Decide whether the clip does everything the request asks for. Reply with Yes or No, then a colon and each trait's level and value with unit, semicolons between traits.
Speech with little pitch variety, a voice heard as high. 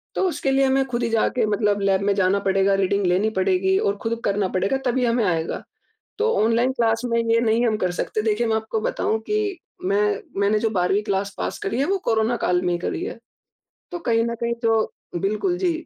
No: average, 3.1 semitones; high, 220 Hz